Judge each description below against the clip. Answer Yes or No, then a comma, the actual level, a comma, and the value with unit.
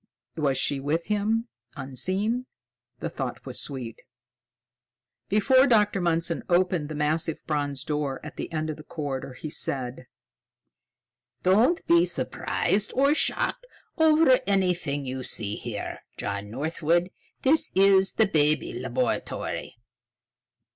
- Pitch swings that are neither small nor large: No, wide, 6.2 semitones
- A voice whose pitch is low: No, medium, 165 Hz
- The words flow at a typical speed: No, slow, 120 wpm